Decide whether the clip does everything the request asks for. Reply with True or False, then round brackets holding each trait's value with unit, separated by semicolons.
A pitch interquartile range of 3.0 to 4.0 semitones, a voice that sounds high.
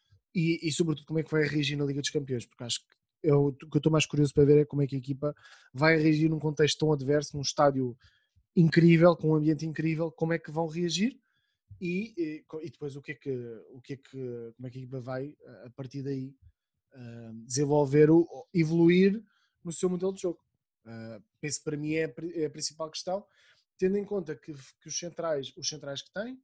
False (3.3 semitones; 155 Hz)